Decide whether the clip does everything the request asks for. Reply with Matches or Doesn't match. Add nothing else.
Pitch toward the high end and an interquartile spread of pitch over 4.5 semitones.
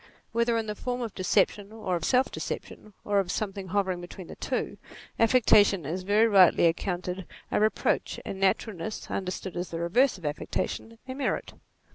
Doesn't match